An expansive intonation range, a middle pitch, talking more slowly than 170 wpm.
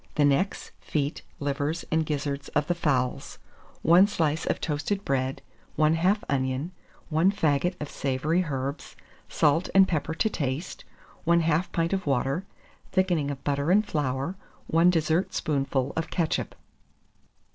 No: average, 3.7 semitones; medium, 155 Hz; slow, 135 wpm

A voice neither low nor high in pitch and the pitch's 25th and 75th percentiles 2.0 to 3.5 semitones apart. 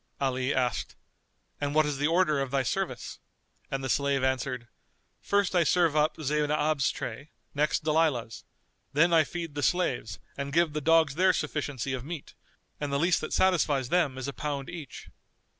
Yes: medium, 145 Hz; average, 3.1 semitones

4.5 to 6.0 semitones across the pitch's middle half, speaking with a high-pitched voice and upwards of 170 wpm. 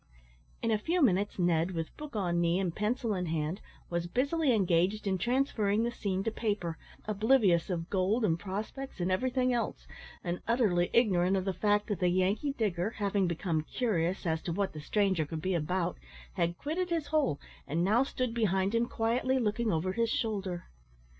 Yes: average, 4.8 semitones; high, 200 Hz; average, 185 wpm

